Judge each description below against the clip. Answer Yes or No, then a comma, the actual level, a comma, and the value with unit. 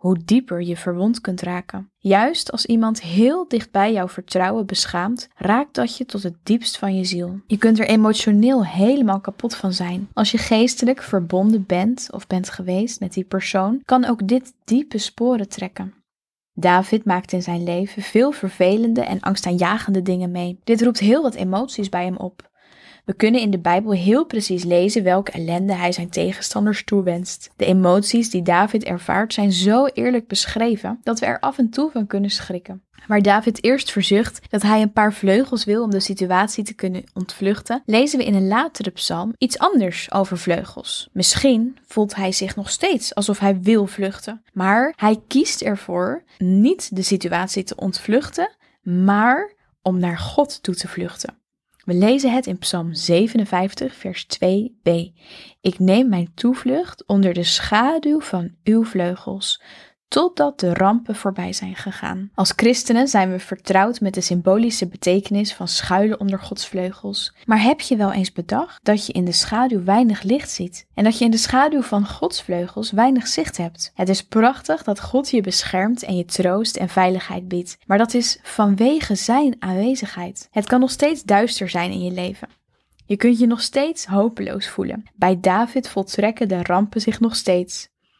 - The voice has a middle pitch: No, high, 205 Hz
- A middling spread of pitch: Yes, average, 4.1 semitones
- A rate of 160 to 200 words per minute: Yes, average, 175 wpm